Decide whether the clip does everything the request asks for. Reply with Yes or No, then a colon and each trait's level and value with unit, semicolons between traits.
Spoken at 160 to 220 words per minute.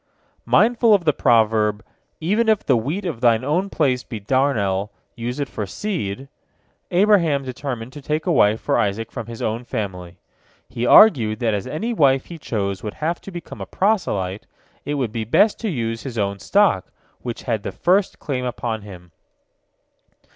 Yes: average, 175 wpm